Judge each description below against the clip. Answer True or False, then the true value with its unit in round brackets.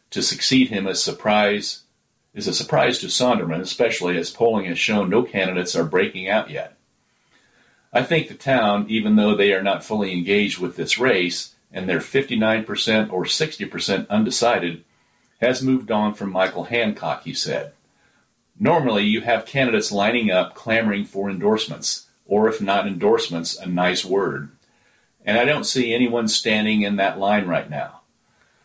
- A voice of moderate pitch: False (105 Hz)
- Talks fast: False (160 wpm)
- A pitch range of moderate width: True (3.0 semitones)